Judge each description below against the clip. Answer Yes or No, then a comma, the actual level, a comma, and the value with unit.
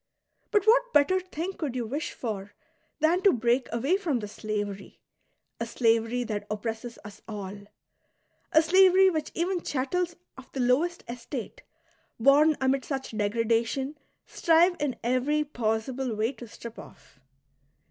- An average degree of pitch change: No, wide, 6.0 semitones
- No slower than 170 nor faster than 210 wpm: No, average, 145 wpm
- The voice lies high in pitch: Yes, very high, 255 Hz